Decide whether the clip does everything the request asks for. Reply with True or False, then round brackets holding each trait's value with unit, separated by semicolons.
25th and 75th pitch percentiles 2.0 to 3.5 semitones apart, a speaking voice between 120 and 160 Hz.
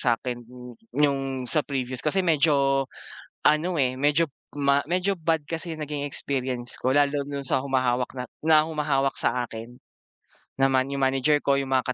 True (2.7 semitones; 140 Hz)